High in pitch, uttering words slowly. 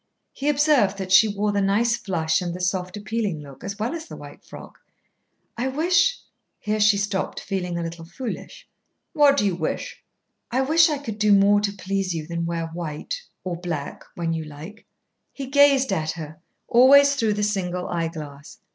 No: high, 200 Hz; average, 190 wpm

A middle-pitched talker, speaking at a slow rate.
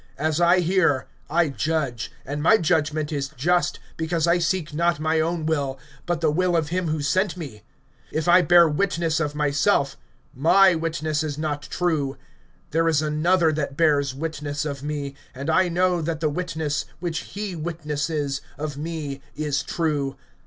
No: medium, 155 Hz; average, 165 wpm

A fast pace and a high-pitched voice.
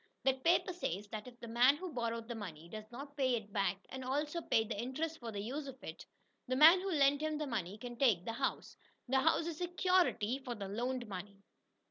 Yes: fast, 220 wpm; very high, 250 Hz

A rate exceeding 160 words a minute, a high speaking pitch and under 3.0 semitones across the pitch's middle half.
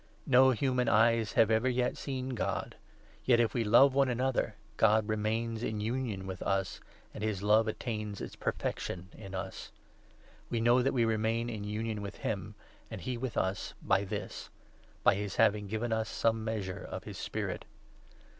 No: average, 180 wpm; low, 110 Hz; narrow, 2.4 semitones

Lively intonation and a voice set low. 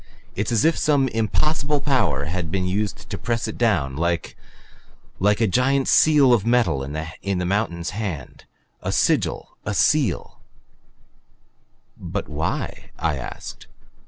Yes: wide, 6.6 semitones; low, 105 Hz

